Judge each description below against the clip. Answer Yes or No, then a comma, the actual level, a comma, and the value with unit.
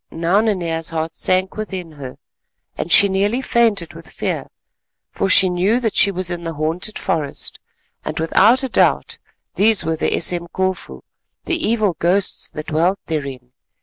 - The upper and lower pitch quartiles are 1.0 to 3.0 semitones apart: No, average, 3.7 semitones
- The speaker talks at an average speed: Yes, average, 155 wpm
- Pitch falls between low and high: Yes, medium, 180 Hz